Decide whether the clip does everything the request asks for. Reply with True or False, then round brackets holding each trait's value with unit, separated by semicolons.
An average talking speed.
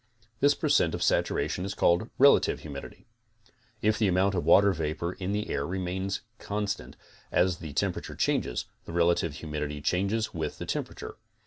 True (160 wpm)